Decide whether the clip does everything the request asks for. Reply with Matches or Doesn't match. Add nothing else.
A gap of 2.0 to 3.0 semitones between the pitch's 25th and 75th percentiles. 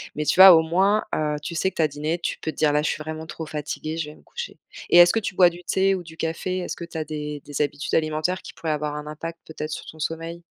Matches